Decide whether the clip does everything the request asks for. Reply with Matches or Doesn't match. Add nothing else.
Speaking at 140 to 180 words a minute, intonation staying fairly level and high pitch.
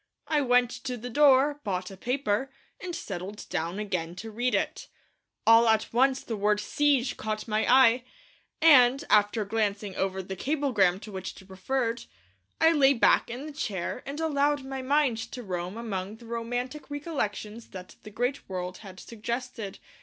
Doesn't match